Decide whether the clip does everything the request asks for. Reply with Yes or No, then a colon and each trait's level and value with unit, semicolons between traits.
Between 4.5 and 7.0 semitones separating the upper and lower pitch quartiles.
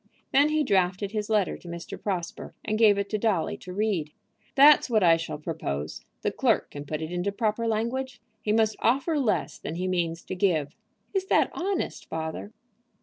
Yes: average, 5.1 semitones